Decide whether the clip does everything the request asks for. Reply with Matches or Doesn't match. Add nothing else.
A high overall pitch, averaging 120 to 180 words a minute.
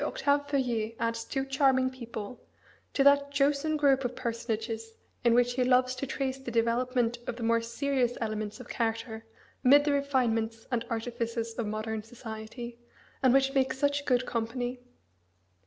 Matches